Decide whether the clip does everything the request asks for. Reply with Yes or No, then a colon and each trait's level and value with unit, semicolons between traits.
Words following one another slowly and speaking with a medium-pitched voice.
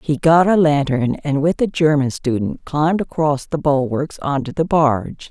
No: average, 190 wpm; medium, 150 Hz